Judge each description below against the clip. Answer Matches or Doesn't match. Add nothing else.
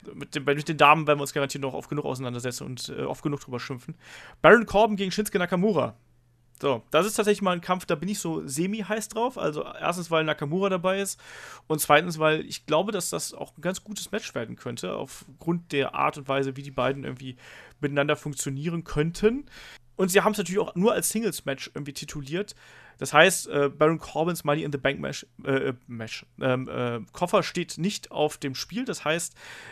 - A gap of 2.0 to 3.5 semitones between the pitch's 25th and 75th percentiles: Doesn't match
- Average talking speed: Doesn't match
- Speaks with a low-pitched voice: Doesn't match